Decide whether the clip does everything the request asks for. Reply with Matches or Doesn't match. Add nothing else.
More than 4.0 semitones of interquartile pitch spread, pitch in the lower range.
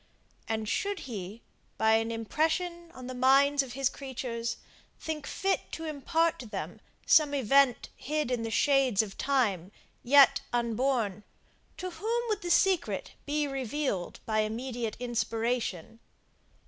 Doesn't match